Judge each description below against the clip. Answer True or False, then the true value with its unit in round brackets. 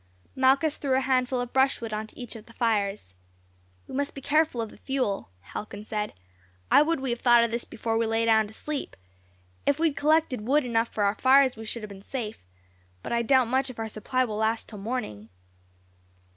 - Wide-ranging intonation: False (3.5 semitones)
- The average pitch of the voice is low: False (235 Hz)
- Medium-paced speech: False (215 wpm)